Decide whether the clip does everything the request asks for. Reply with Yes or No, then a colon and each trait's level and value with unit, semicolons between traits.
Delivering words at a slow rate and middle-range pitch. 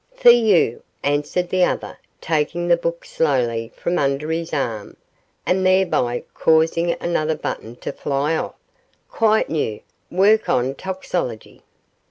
Yes: slow, 130 wpm; medium, 160 Hz